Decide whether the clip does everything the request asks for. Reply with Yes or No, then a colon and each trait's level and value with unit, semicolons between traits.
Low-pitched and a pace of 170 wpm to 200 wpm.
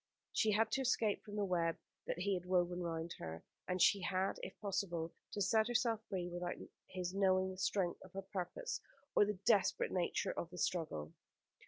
No: medium, 185 Hz; average, 190 wpm